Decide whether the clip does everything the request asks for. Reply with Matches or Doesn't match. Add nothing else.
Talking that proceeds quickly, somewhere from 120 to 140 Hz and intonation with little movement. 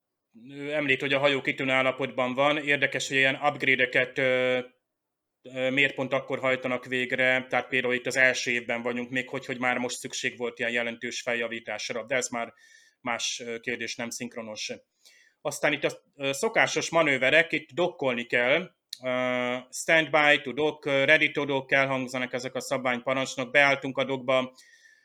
Doesn't match